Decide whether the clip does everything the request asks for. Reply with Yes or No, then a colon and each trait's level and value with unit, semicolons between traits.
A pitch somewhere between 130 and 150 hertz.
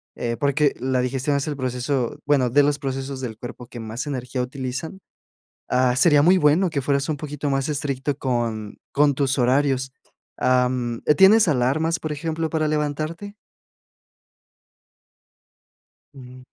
Yes: medium, 140 Hz